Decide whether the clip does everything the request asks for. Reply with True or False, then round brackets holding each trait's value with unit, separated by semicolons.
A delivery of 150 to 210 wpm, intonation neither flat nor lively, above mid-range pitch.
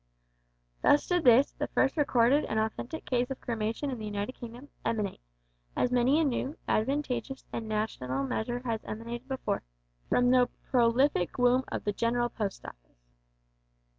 True (155 wpm; 3.3 semitones; 240 Hz)